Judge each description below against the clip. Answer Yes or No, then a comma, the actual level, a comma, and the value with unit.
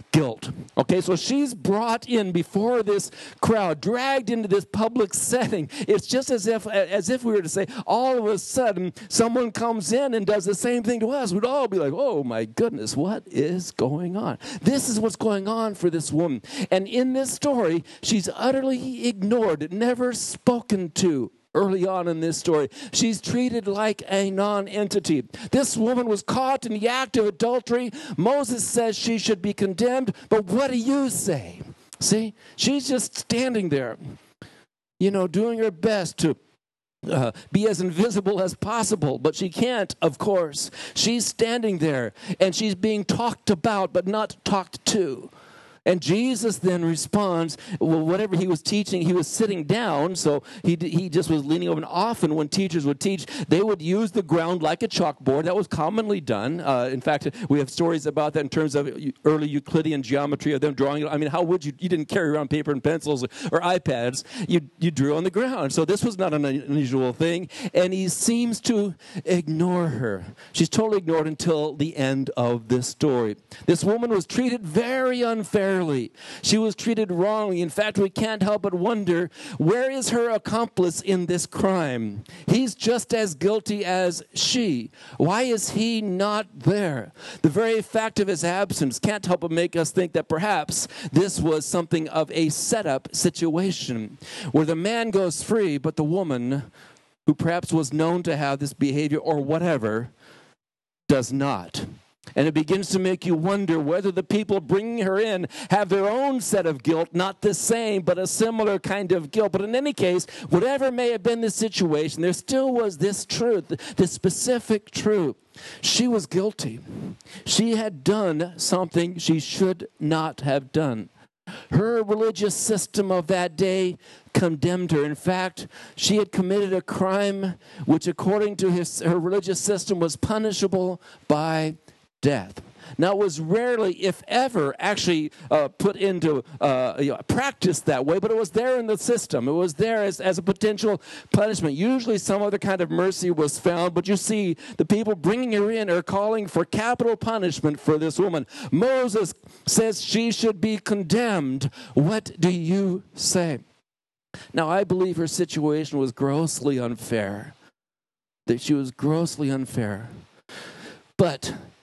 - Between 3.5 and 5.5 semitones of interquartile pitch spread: Yes, average, 5.2 semitones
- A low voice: No, high, 190 Hz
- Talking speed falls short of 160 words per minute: No, average, 175 wpm